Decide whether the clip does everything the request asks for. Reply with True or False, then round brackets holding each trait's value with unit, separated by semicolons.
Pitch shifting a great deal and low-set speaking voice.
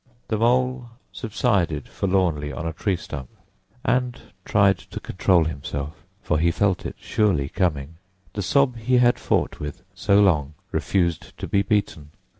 True (5.9 semitones; 95 Hz)